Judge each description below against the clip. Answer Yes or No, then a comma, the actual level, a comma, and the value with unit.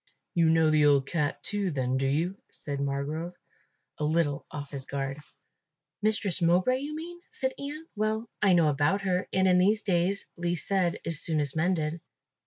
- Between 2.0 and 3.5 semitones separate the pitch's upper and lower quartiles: No, average, 5.1 semitones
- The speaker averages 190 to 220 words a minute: No, average, 175 wpm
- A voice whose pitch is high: No, medium, 170 Hz